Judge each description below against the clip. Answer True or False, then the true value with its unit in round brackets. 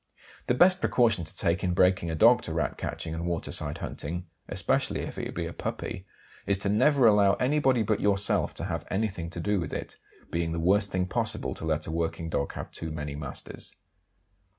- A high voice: False (90 Hz)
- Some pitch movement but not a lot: True (4.0 semitones)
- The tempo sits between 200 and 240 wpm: True (205 wpm)